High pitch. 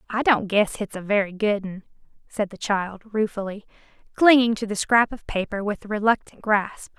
Yes: high, 210 Hz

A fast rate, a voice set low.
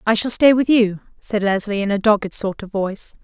No: fast, 240 wpm; high, 210 Hz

